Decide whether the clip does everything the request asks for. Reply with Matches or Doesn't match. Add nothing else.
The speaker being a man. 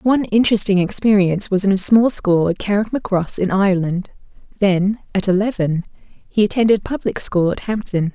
Doesn't match